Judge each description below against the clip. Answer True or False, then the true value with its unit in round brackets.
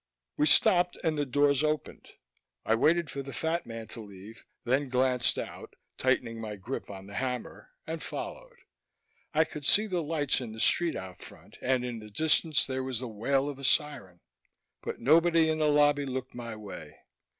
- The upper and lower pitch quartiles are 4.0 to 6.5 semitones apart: True (5.1 semitones)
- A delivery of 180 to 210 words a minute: True (185 wpm)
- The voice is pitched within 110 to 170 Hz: True (135 Hz)